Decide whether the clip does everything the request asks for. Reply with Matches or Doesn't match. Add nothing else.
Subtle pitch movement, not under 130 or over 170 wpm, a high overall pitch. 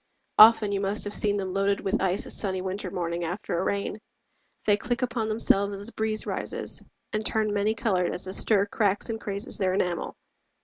Doesn't match